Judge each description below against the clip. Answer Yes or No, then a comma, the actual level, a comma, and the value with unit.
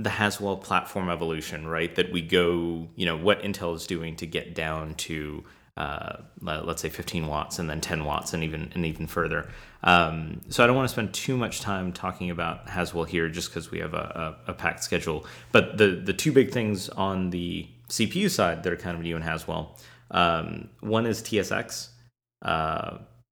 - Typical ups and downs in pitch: Yes, average, 3.7 semitones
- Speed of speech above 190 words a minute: Yes, fast, 205 wpm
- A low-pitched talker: Yes, very low, 85 Hz